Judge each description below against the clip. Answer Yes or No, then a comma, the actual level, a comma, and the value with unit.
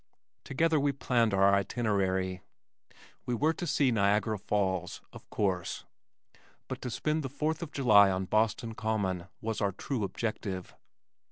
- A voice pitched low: Yes, low, 110 Hz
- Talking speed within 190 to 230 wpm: No, average, 145 wpm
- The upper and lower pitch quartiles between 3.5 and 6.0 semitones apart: Yes, average, 5.2 semitones